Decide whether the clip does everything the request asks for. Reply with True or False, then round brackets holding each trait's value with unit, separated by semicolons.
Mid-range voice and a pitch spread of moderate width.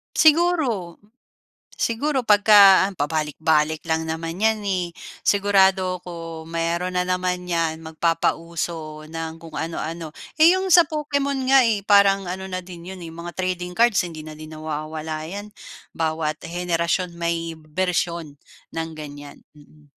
True (170 Hz; 3.5 semitones)